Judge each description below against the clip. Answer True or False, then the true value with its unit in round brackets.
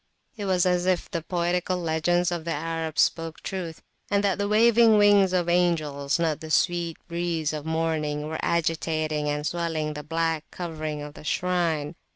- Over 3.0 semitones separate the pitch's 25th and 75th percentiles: False (2.4 semitones)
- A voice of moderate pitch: True (165 Hz)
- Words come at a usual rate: True (175 wpm)